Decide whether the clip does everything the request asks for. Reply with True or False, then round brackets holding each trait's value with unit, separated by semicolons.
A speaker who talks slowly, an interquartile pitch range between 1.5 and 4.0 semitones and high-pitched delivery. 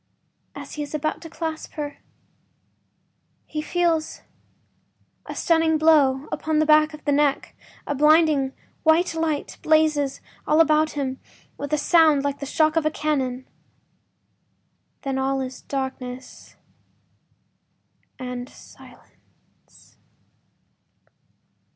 True (110 wpm; 2.5 semitones; 300 Hz)